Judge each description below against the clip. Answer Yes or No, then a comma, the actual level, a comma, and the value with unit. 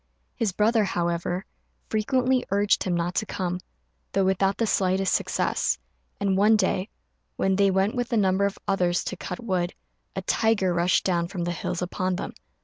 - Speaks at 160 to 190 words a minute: Yes, average, 175 wpm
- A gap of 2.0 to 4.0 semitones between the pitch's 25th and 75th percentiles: Yes, narrow, 2.4 semitones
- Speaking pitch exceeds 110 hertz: Yes, high, 190 Hz